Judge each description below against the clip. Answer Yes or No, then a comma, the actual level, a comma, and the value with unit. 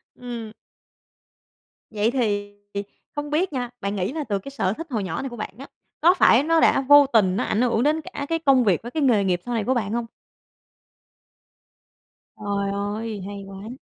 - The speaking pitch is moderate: No, high, 230 Hz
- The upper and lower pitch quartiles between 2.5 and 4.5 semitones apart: No, average, 5.2 semitones